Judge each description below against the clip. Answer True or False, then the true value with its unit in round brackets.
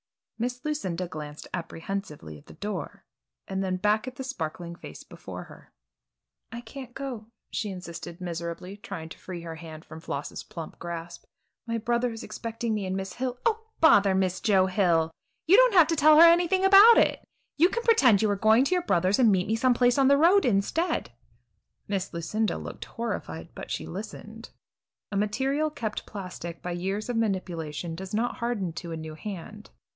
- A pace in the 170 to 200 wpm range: True (190 wpm)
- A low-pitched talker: False (205 Hz)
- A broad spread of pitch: True (6.3 semitones)